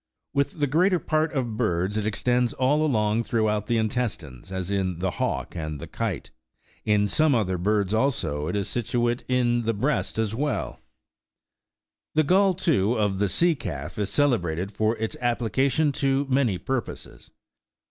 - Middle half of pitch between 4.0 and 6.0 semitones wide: Yes, average, 5.2 semitones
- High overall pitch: No, low, 115 Hz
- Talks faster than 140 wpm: Yes, average, 160 wpm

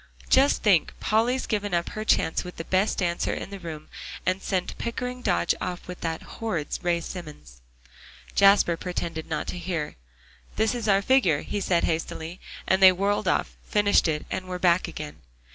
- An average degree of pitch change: Yes, average, 3.6 semitones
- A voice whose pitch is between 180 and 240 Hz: Yes, medium, 185 Hz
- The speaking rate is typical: Yes, average, 180 wpm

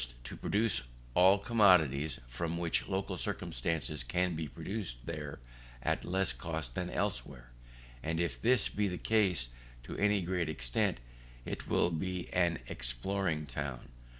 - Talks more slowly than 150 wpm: Yes, average, 140 wpm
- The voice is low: Yes, very low, 85 Hz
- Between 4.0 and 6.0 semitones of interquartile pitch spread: Yes, average, 5.2 semitones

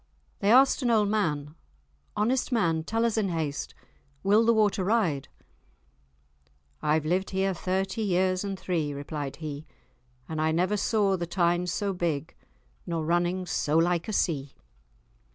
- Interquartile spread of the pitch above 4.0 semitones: Yes, average, 4.4 semitones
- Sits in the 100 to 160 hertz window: No, medium, 180 Hz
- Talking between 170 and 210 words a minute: No, average, 150 wpm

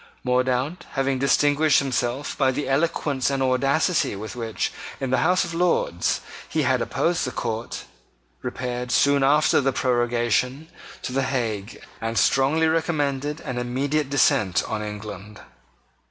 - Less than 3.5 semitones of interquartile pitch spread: Yes, average, 3.1 semitones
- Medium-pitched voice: No, low, 130 Hz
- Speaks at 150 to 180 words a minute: No, average, 140 wpm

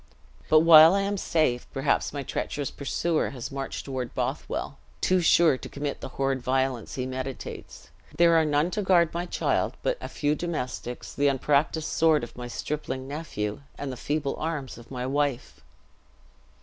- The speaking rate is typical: Yes, average, 170 wpm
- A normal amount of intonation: Yes, average, 3.7 semitones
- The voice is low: No, medium, 145 Hz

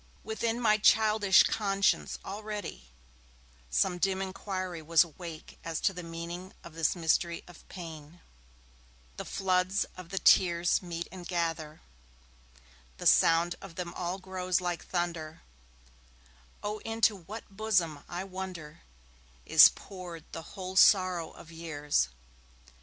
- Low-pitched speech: No, medium, 180 Hz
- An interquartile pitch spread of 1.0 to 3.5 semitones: Yes, narrow, 2.6 semitones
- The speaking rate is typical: No, slow, 125 wpm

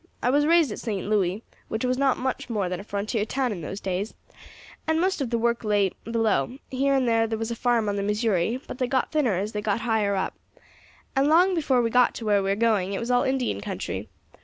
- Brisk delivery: Yes, fast, 245 wpm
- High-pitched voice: Yes, high, 230 Hz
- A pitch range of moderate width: Yes, average, 3.8 semitones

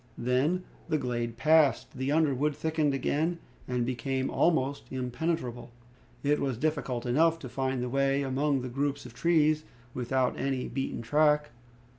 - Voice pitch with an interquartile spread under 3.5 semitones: Yes, average, 3.1 semitones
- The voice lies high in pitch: No, low, 135 Hz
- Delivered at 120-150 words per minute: Yes, average, 145 wpm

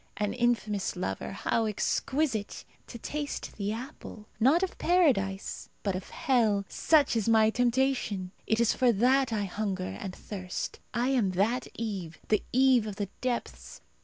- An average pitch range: Yes, average, 4.2 semitones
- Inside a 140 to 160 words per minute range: Yes, average, 155 wpm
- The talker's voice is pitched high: Yes, high, 220 Hz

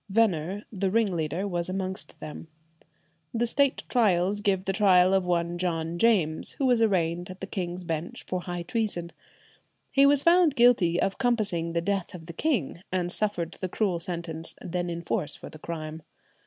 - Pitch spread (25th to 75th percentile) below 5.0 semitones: Yes, average, 3.7 semitones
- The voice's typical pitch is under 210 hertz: Yes, medium, 185 Hz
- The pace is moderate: Yes, average, 175 wpm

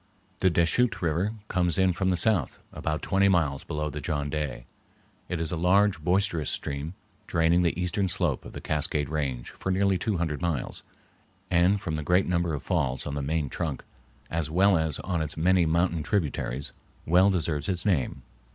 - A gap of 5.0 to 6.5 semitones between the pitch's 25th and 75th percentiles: No, average, 3.4 semitones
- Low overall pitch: Yes, very low, 85 Hz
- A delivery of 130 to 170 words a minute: No, average, 185 wpm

